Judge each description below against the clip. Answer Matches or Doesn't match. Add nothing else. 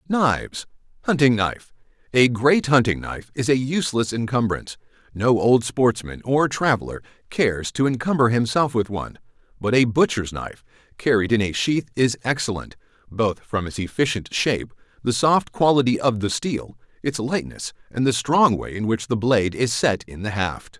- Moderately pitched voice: Doesn't match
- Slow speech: Doesn't match